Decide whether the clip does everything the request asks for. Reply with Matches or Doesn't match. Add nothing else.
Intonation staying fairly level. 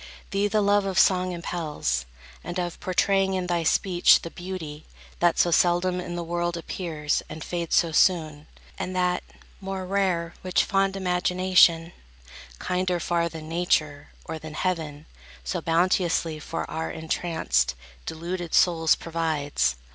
Matches